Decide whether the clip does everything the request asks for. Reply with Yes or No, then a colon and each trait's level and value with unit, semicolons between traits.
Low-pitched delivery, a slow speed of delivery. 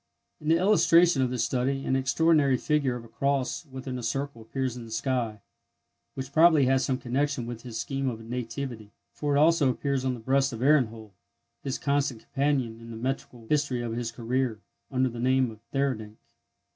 No: low, 130 Hz; average, 190 wpm